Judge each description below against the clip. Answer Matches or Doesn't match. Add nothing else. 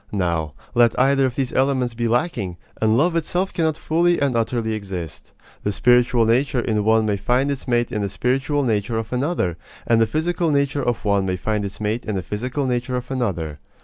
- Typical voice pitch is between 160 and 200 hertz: Doesn't match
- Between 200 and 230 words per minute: Matches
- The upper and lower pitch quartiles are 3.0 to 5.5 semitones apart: Matches